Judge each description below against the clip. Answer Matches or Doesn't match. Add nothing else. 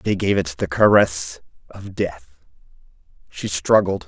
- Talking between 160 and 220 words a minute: Doesn't match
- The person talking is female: Doesn't match